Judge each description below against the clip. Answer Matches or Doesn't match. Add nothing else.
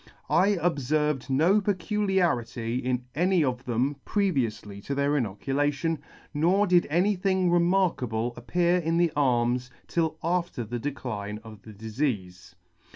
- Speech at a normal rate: Doesn't match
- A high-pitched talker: Doesn't match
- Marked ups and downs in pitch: Matches